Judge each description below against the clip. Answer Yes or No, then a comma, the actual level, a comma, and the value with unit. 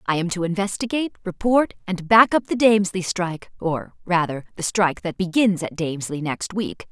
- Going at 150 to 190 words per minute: Yes, average, 180 wpm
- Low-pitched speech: No, medium, 185 Hz